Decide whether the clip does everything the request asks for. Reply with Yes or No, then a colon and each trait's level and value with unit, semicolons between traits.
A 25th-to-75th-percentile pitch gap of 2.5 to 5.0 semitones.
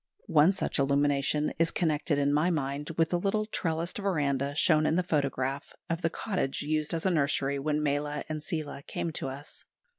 Yes: average, 2.8 semitones